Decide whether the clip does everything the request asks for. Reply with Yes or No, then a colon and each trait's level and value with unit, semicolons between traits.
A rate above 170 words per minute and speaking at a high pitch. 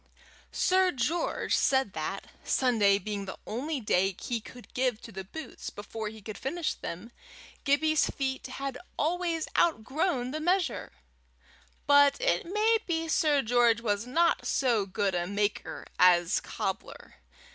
No: average, 140 wpm; very high, 250 Hz